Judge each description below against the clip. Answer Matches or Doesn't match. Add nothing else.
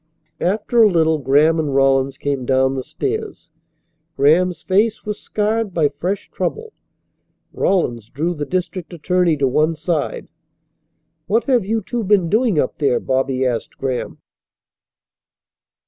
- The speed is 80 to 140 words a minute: Matches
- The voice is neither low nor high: Matches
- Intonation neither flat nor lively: Doesn't match